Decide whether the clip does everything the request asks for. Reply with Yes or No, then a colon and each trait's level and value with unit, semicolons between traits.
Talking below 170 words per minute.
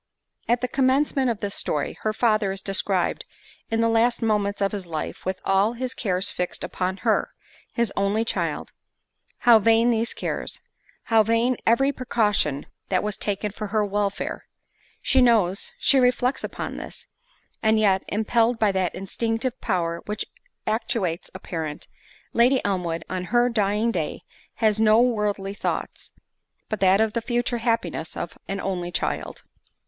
Yes: average, 155 wpm